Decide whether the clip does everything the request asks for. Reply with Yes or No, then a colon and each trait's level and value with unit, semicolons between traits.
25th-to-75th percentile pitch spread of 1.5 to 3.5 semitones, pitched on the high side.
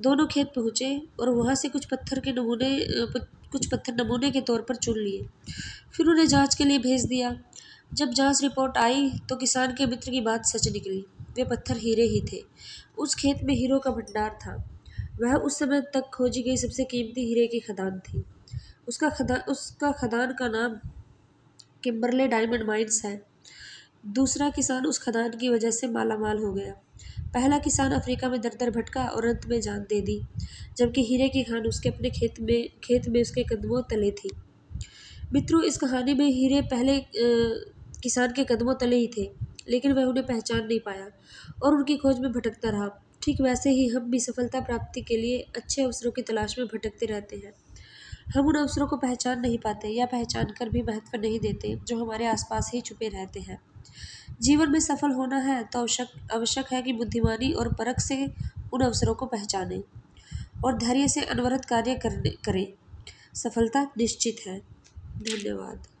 Yes: average, 2.9 semitones; high, 245 Hz